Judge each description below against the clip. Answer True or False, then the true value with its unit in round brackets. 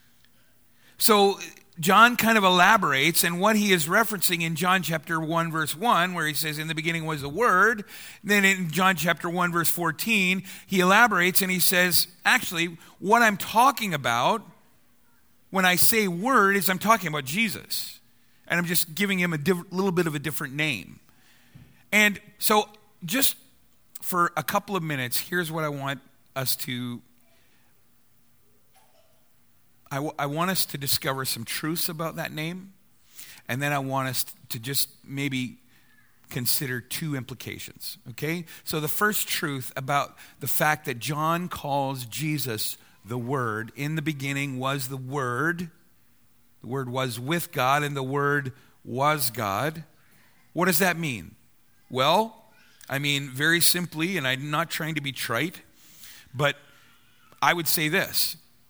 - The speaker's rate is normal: True (155 wpm)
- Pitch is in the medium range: True (160 Hz)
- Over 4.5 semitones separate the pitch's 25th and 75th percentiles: True (4.9 semitones)